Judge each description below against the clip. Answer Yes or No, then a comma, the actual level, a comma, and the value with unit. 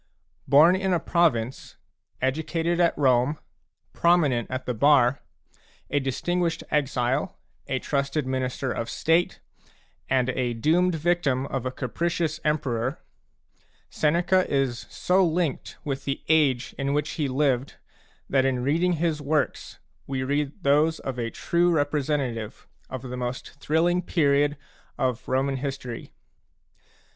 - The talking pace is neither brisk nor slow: No, slow, 130 wpm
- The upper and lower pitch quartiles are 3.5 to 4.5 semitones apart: Yes, average, 3.9 semitones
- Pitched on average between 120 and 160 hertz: Yes, medium, 140 Hz